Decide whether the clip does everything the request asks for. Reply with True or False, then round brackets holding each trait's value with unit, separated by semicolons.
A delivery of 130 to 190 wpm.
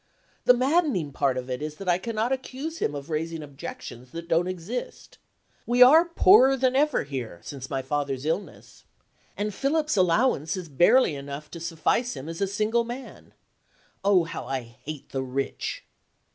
True (170 wpm)